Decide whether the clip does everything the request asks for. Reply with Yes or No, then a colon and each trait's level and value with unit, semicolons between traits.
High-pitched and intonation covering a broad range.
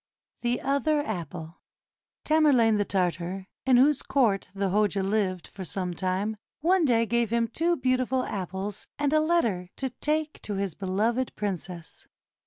Yes: high, 215 Hz; wide, 5.8 semitones